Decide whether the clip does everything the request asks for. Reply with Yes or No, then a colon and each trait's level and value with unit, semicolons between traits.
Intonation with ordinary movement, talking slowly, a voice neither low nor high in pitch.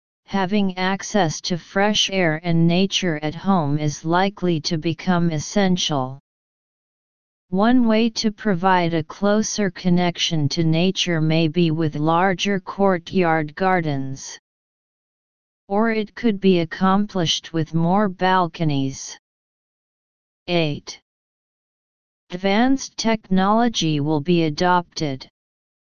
Yes: average, 3.4 semitones; slow, 100 wpm; medium, 180 Hz